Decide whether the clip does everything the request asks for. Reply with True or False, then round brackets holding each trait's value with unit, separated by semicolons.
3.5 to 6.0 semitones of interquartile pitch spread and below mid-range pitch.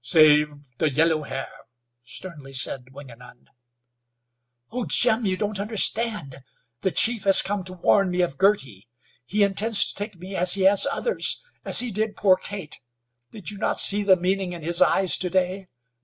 False (5.1 semitones; 185 Hz)